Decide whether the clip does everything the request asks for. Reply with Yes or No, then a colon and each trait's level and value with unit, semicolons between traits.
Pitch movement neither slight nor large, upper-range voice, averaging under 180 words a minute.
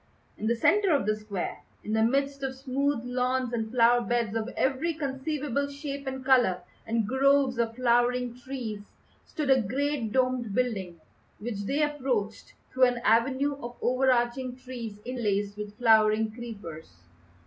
Yes: average, 3.2 semitones; high, 245 Hz; average, 150 wpm